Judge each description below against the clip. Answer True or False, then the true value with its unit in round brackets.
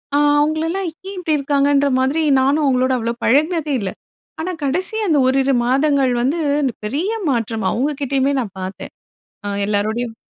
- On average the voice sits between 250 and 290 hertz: True (275 Hz)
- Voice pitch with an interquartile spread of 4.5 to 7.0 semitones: False (3.9 semitones)